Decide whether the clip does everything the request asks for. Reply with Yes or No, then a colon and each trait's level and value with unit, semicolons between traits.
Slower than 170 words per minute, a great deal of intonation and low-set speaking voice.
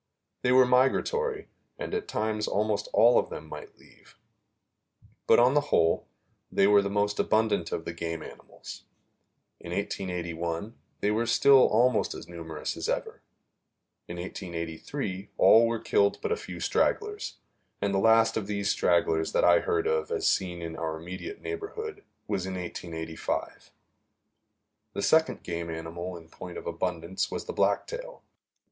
Yes: average, 155 wpm; wide, 6.8 semitones; low, 100 Hz